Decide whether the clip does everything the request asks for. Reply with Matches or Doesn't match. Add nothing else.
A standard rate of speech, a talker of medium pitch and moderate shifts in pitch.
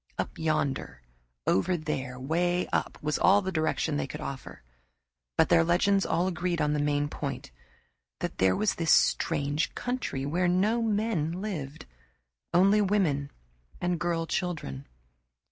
Matches